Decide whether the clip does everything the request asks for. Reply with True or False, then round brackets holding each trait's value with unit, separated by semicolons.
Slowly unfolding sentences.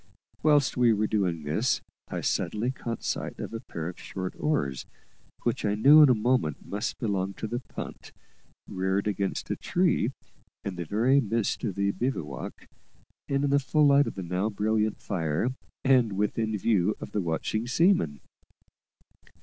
False (165 wpm)